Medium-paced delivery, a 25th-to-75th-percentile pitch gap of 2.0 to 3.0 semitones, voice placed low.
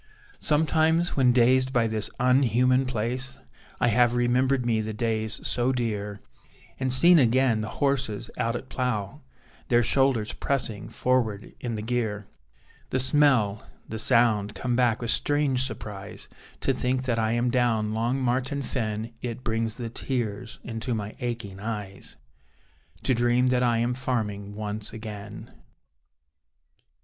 Yes: average, 145 wpm; average, 2.7 semitones; low, 120 Hz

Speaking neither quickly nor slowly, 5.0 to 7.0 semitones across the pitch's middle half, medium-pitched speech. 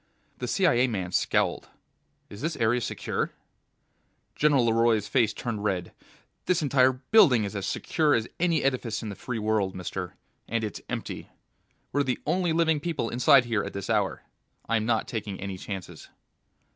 No: average, 160 wpm; average, 5.3 semitones; low, 115 Hz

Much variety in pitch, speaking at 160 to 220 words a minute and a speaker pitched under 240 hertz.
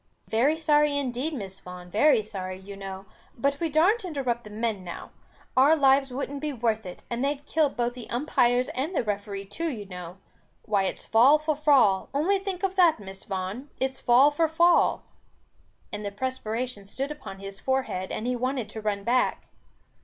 No: wide, 6.1 semitones; average, 185 wpm; very high, 250 Hz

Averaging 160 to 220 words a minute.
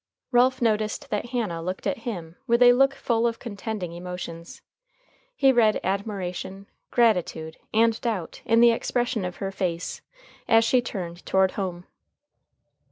No: average, 145 wpm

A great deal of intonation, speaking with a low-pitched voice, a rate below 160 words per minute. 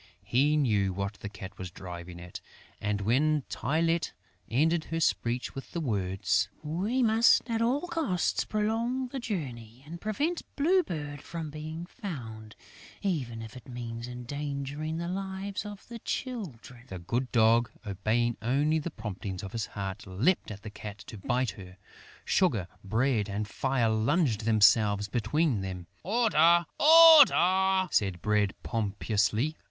Yes: wide, 8.5 semitones; low, 125 Hz; average, 145 wpm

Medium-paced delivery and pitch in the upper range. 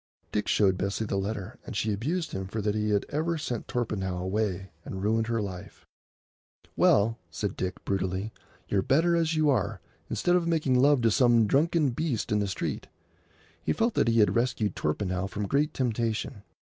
No: average, 180 wpm; low, 110 Hz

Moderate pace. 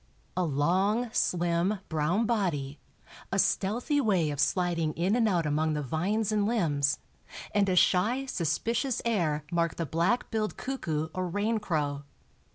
Yes: average, 145 wpm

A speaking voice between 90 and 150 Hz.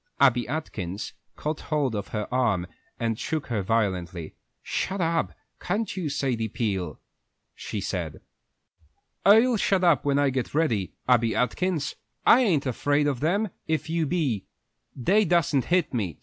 Yes: medium, 140 Hz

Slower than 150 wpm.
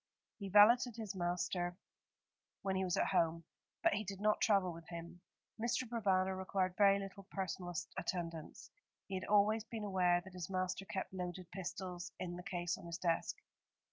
No: average, 170 wpm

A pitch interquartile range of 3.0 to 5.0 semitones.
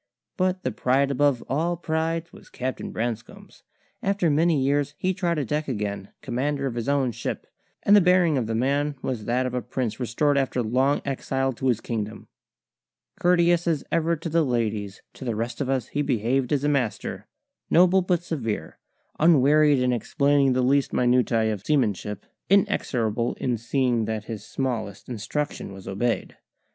Yes: average, 4.4 semitones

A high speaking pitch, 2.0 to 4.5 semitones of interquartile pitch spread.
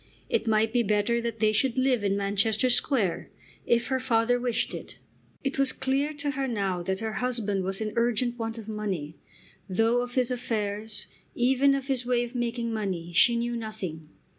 Yes: high, 230 Hz; average, 3.1 semitones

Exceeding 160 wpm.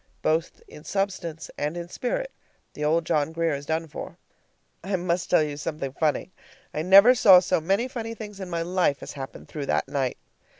Yes: average, 195 wpm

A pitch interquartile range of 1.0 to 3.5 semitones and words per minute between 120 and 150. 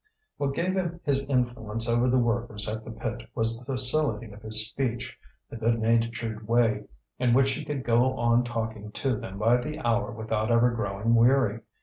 No: narrow, 2.4 semitones; average, 190 wpm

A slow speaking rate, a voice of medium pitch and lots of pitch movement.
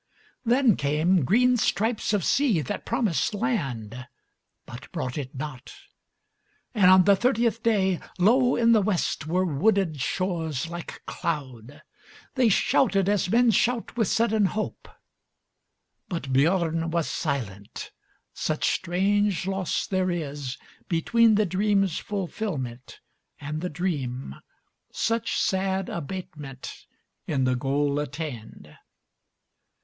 Yes: slow, 105 wpm; medium, 180 Hz; wide, 6.3 semitones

